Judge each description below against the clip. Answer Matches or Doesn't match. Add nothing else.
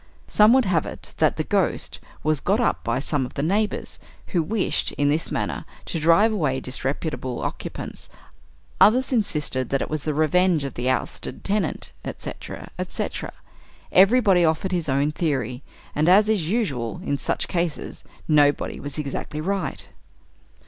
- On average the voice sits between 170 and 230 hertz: Doesn't match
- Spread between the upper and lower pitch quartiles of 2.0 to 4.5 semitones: Doesn't match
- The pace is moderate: Matches